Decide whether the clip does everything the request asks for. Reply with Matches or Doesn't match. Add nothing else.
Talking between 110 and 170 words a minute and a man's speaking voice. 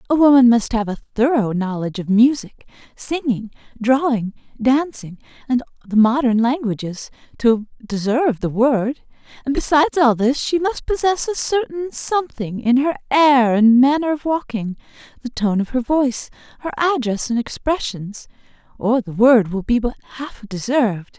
Doesn't match